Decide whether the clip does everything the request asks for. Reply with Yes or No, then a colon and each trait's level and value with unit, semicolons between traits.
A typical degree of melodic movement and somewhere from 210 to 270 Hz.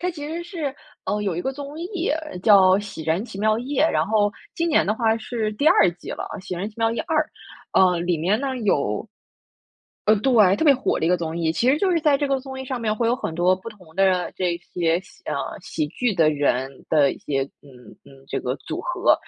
No: wide, 7.5 semitones; high, 215 Hz